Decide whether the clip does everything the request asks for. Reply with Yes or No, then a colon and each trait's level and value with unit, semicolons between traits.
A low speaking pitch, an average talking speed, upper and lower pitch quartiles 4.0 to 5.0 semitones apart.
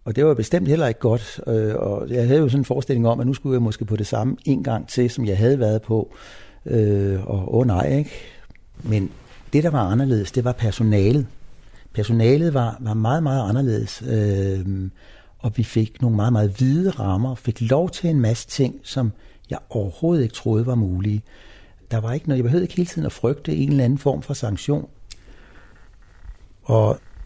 Yes: low, 115 Hz; average, 195 wpm; average, 4.3 semitones